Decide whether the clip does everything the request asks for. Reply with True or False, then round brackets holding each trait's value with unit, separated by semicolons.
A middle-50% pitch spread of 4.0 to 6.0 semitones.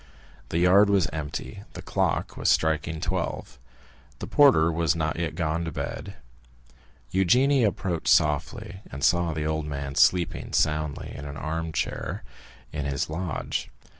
False (3.3 semitones)